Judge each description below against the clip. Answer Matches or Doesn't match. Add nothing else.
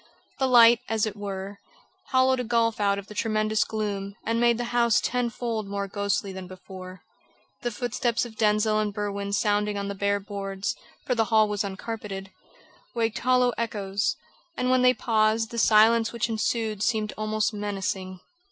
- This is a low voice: Doesn't match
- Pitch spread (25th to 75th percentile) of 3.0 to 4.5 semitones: Doesn't match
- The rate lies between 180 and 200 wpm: Doesn't match